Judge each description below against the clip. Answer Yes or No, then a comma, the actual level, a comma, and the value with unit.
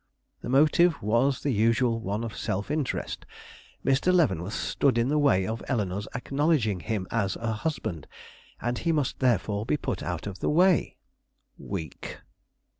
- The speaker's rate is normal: Yes, average, 155 wpm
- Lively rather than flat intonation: Yes, wide, 5.9 semitones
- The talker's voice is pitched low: Yes, low, 115 Hz